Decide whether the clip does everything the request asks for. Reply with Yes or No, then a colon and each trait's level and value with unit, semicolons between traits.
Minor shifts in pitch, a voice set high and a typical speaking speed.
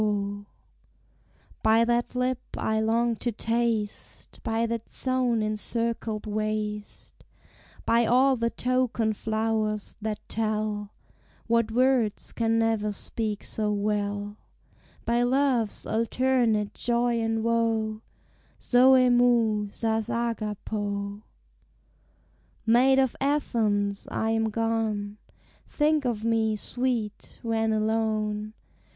No: narrow, 1.9 semitones; high, 225 Hz; slow, 105 wpm